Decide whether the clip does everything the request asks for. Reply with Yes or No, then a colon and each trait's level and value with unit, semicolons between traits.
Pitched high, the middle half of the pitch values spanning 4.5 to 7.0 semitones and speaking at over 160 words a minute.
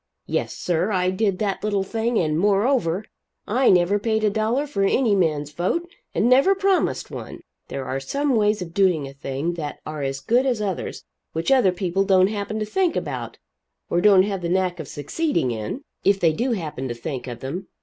Yes: high, 195 Hz; average, 5.1 semitones; average, 200 wpm